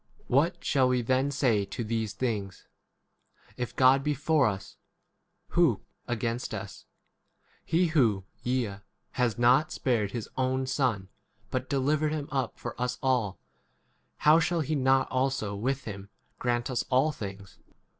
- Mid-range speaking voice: No, low, 130 Hz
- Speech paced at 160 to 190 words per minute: No, average, 150 wpm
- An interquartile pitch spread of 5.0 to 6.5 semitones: No, average, 3.4 semitones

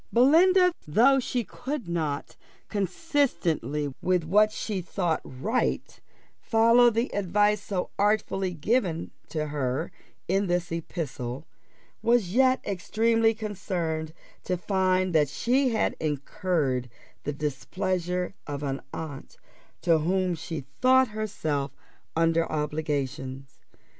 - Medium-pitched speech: Yes, medium, 180 Hz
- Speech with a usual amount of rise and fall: No, wide, 6.1 semitones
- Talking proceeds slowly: Yes, slow, 110 wpm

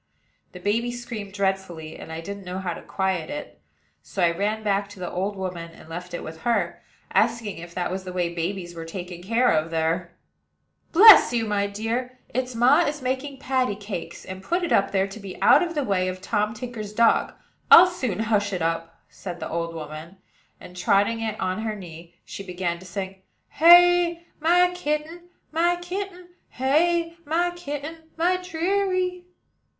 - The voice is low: No, high, 205 Hz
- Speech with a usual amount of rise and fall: No, wide, 8.4 semitones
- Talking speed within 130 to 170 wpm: No, average, 185 wpm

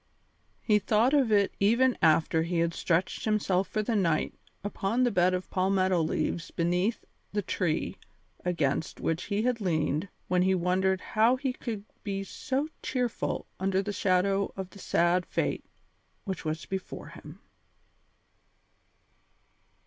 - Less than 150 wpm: Yes, average, 140 wpm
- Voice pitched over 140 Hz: Yes, high, 190 Hz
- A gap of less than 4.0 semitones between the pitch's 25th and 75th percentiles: Yes, average, 3.2 semitones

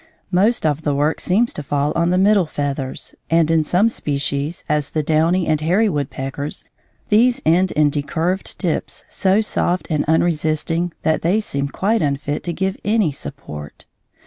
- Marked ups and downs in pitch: No, average, 4.2 semitones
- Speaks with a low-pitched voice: No, medium, 160 Hz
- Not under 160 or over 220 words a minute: Yes, average, 170 wpm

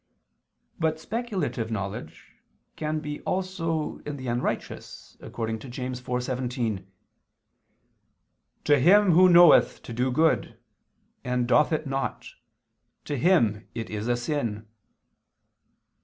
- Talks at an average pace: No, slow, 110 wpm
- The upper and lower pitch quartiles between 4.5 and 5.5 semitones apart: Yes, average, 5.1 semitones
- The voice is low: Yes, low, 130 Hz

